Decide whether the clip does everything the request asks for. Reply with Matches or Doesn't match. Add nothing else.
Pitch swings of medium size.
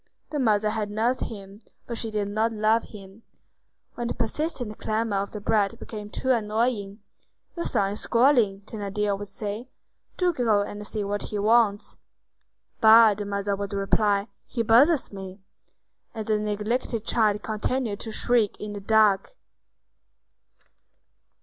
Doesn't match